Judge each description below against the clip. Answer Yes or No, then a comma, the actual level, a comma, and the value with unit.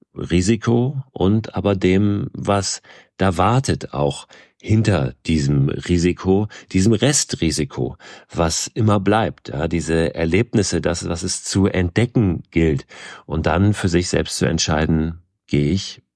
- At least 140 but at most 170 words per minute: No, slow, 125 wpm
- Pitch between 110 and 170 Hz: No, very low, 95 Hz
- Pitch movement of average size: Yes, average, 4.1 semitones